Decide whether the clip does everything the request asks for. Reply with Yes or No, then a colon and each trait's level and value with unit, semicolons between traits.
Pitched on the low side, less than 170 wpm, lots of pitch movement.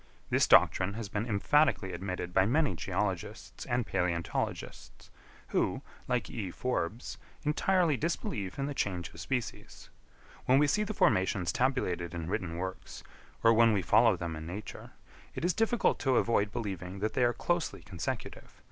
Yes: low, 105 Hz; average, 155 wpm; wide, 6.3 semitones